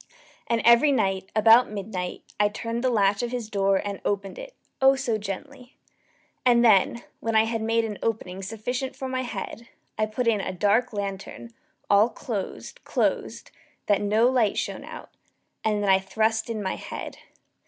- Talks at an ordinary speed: Yes, average, 175 wpm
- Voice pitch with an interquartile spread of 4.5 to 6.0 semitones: No, average, 2.9 semitones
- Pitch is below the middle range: No, high, 220 Hz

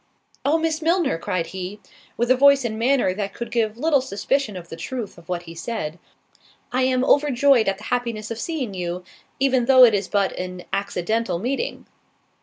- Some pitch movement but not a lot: No, wide, 5.8 semitones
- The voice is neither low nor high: No, high, 230 Hz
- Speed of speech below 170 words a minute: No, average, 190 wpm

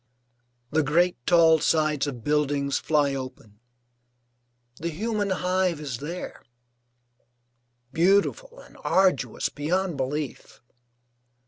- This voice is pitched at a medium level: Yes, medium, 155 Hz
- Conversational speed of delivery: No, slow, 95 wpm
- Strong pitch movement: No, average, 4.1 semitones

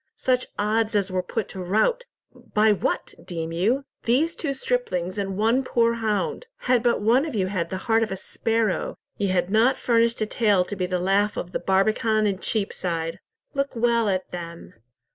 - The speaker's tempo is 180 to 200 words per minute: Yes, average, 185 wpm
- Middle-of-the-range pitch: No, high, 215 Hz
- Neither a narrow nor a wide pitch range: Yes, average, 3.9 semitones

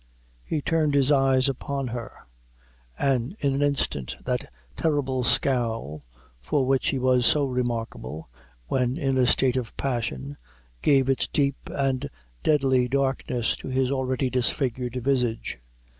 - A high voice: No, low, 130 Hz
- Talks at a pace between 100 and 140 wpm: Yes, slow, 135 wpm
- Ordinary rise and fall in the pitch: No, narrow, 2.1 semitones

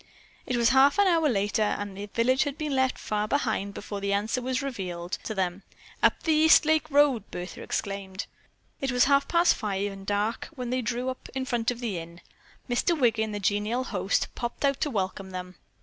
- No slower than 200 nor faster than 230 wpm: Yes, fast, 205 wpm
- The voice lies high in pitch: Yes, high, 230 Hz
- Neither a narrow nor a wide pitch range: Yes, average, 4.9 semitones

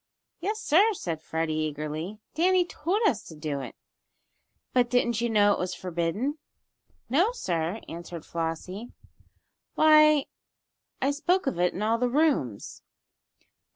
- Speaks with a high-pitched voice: Yes, high, 220 Hz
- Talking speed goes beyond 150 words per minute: No, slow, 135 wpm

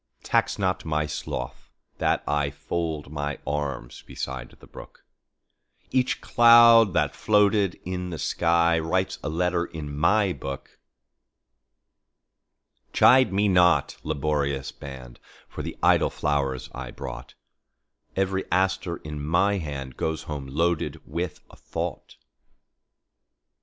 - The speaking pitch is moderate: No, very low, 80 Hz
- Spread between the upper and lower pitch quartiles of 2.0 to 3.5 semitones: No, average, 4.7 semitones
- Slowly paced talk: Yes, slow, 100 wpm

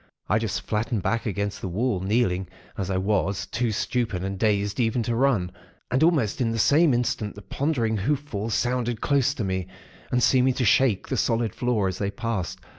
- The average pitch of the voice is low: Yes, low, 110 Hz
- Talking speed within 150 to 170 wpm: No, average, 195 wpm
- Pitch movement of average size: Yes, average, 3.8 semitones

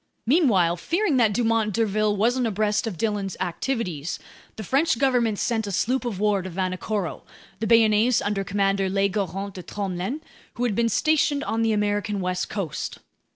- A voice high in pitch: Yes, high, 210 Hz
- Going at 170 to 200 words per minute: No, average, 160 wpm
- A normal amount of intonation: Yes, average, 3.1 semitones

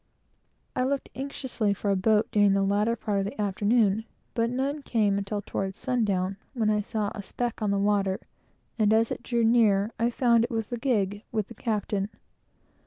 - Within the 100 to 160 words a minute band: No, average, 190 wpm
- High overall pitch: Yes, high, 215 Hz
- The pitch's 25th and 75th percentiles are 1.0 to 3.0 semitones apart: Yes, average, 2.7 semitones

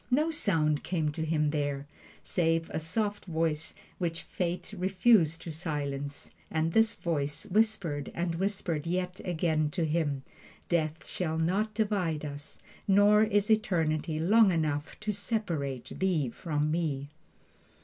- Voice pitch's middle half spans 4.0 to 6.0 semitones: Yes, average, 4.3 semitones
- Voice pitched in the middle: Yes, medium, 165 Hz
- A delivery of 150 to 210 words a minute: No, slow, 135 wpm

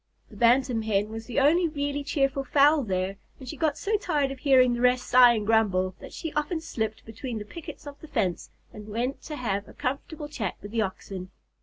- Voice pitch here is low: No, very high, 250 Hz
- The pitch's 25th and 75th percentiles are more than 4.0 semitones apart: Yes, average, 4.9 semitones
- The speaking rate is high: Yes, fast, 215 wpm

